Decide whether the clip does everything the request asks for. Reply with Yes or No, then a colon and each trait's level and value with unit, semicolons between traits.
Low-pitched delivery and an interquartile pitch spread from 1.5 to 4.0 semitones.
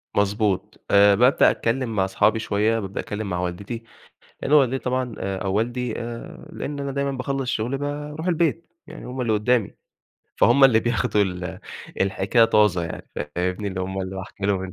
No: low, 110 Hz; average, 4.8 semitones